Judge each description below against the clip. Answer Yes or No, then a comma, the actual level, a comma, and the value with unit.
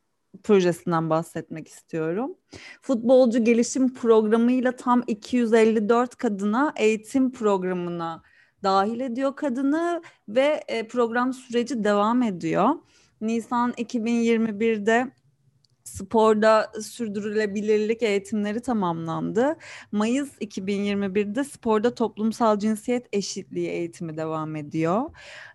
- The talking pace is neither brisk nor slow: No, slow, 80 wpm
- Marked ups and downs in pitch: No, average, 3.5 semitones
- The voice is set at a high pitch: Yes, high, 220 Hz